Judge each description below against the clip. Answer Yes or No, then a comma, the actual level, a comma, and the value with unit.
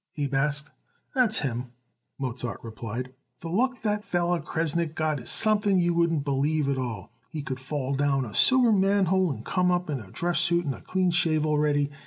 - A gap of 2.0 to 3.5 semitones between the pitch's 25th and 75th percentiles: No, average, 4.7 semitones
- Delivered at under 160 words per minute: No, average, 195 wpm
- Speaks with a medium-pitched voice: Yes, medium, 155 Hz